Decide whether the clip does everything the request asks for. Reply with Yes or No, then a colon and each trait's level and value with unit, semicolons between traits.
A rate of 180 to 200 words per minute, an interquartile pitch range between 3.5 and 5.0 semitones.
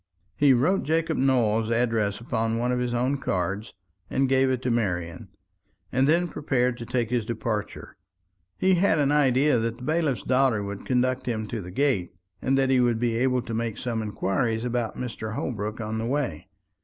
No: average, 190 wpm; average, 3.0 semitones